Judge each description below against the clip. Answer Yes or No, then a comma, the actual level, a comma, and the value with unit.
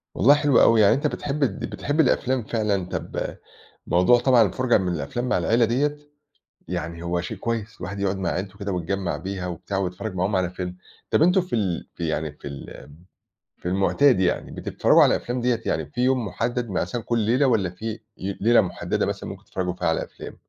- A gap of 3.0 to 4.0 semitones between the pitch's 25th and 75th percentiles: No, average, 5.0 semitones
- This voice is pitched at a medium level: No, low, 100 Hz